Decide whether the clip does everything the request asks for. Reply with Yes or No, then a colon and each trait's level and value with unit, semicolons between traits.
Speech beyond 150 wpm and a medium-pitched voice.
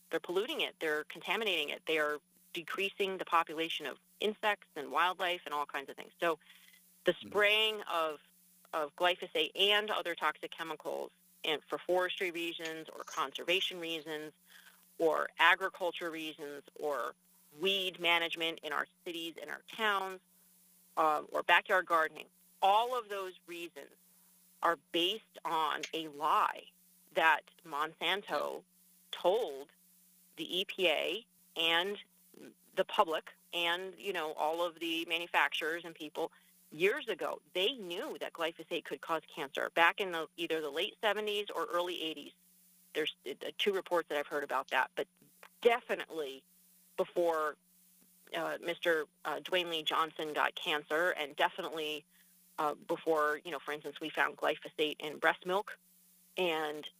No: average, 140 wpm; medium, 175 Hz